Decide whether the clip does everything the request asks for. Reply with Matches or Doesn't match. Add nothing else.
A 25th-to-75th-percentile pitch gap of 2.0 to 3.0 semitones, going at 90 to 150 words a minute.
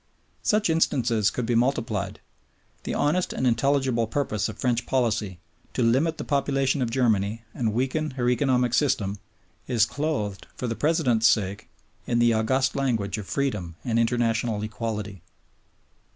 Doesn't match